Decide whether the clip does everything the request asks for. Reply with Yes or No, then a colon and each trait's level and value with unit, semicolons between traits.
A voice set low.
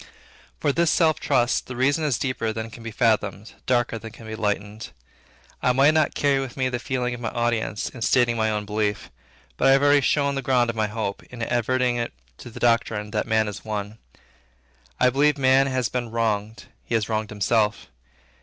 Yes: low, 120 Hz